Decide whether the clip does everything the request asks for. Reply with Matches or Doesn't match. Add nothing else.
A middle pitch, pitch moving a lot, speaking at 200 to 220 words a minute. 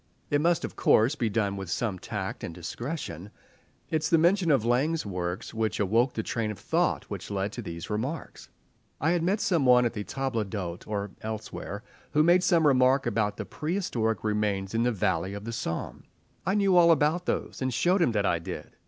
Doesn't match